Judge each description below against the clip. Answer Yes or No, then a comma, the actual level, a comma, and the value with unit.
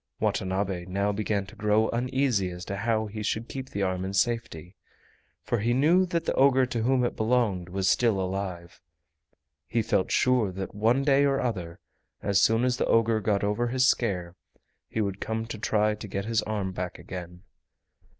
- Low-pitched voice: Yes, low, 105 Hz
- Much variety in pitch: No, average, 3.9 semitones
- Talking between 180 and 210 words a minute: Yes, average, 190 wpm